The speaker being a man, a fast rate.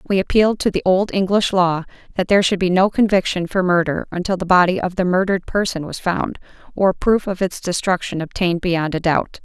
No: female; fast, 210 wpm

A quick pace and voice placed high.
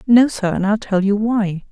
Yes: fast, 245 wpm; high, 210 Hz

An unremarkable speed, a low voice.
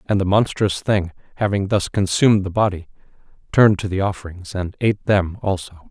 Yes: average, 175 wpm; very low, 95 Hz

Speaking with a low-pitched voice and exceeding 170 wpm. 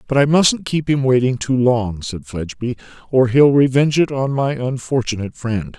Yes: low, 130 Hz; average, 185 wpm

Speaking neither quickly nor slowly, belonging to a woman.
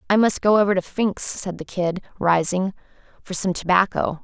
Yes: average, 185 wpm; female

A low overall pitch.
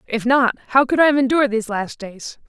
No: high, 245 Hz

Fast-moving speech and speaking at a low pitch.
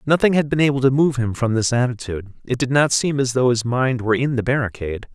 Yes: fast, 255 wpm; low, 125 Hz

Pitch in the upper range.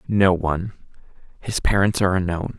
No: very low, 95 Hz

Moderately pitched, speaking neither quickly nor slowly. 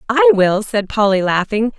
No: high, 220 Hz; average, 170 wpm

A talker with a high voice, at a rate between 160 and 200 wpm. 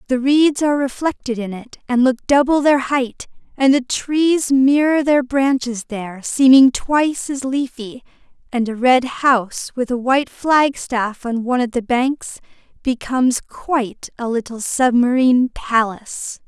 No: very high, 255 Hz; average, 150 wpm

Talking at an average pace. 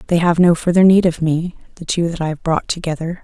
No: fast, 260 wpm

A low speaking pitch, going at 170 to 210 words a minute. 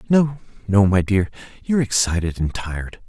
No: low, 105 Hz; average, 155 wpm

